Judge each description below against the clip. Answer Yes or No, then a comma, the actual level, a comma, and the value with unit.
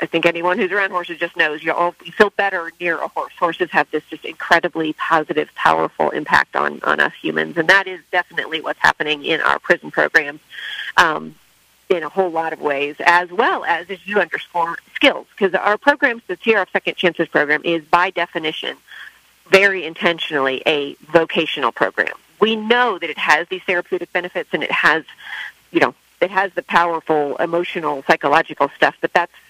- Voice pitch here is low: No, medium, 170 Hz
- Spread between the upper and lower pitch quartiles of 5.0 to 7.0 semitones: No, average, 3.1 semitones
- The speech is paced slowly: No, average, 180 wpm